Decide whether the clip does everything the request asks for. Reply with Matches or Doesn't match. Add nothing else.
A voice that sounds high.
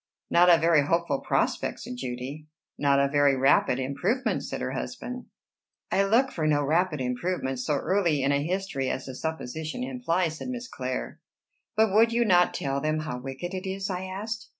Doesn't match